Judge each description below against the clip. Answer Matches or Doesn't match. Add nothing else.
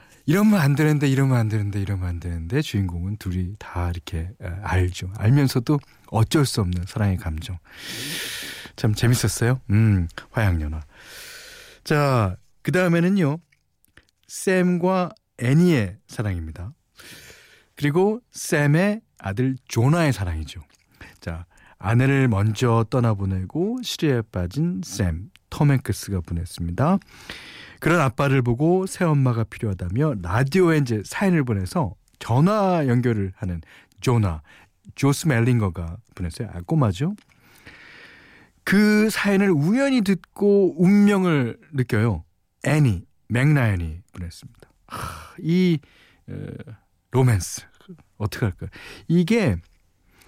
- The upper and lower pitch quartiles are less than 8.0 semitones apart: Doesn't match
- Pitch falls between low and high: Doesn't match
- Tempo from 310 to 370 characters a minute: Doesn't match